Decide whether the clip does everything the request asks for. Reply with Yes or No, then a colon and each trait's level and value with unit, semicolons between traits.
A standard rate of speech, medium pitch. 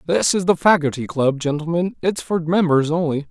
Yes: average, 180 wpm; medium, 165 Hz